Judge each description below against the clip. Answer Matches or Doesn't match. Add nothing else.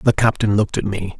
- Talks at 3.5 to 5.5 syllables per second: Doesn't match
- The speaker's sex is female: Doesn't match